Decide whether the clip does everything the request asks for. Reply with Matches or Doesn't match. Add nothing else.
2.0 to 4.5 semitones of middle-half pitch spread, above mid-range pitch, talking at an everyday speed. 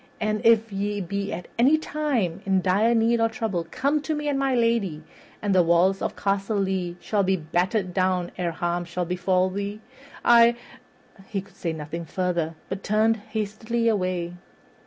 Matches